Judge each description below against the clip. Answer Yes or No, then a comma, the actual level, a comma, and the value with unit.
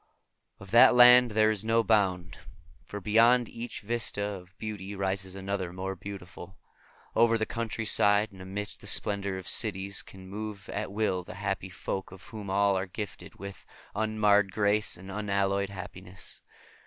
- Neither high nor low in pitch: No, low, 100 Hz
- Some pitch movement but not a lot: No, narrow, 2.2 semitones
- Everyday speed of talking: Yes, average, 155 wpm